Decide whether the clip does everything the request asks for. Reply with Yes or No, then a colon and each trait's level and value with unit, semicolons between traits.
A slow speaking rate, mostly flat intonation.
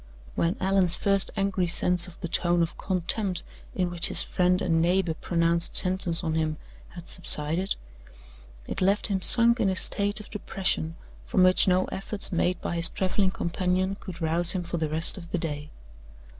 No: average, 180 wpm; narrow, 2.2 semitones